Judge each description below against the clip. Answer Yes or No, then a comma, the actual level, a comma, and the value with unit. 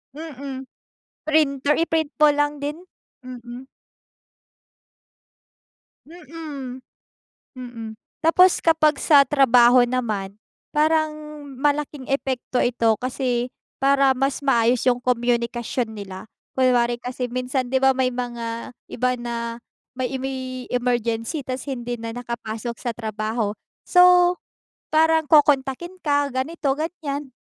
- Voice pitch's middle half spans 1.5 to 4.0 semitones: Yes, average, 3.4 semitones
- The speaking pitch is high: Yes, very high, 255 Hz